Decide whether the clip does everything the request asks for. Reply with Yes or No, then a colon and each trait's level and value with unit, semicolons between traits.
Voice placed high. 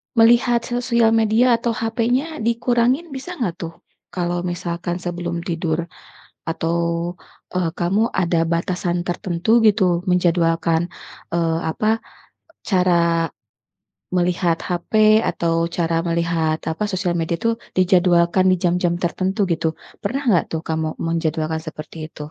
No: medium, 175 Hz